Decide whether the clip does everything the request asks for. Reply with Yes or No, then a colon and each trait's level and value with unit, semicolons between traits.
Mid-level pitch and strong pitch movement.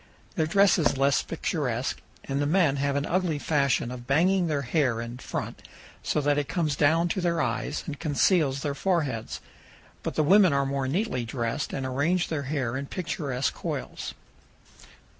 No: medium, 145 Hz; average, 3.6 semitones